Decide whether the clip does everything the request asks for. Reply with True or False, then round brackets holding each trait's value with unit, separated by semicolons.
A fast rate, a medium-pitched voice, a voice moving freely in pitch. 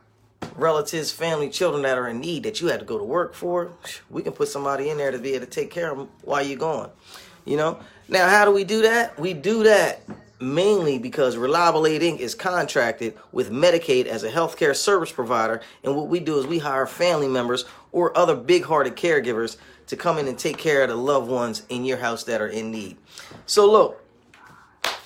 True (215 wpm; 155 Hz; 8.6 semitones)